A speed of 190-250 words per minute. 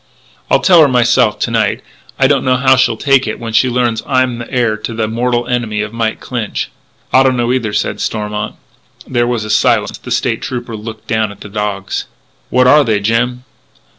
Yes: fast, 205 wpm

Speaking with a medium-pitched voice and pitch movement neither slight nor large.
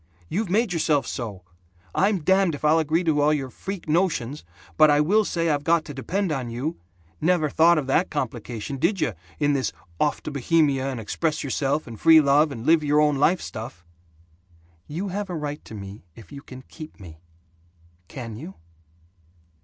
Yes: medium, 150 Hz; average, 3.9 semitones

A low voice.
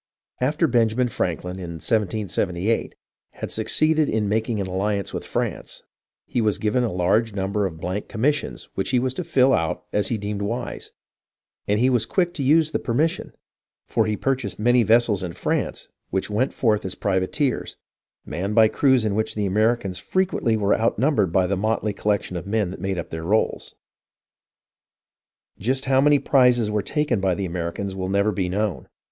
Yes: low, 105 Hz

